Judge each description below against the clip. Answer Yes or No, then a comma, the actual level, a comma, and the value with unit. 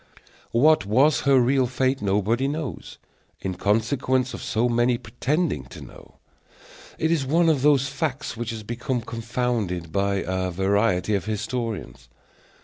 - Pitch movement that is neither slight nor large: Yes, average, 4.9 semitones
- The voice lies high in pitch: No, low, 120 Hz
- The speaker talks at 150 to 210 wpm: No, average, 140 wpm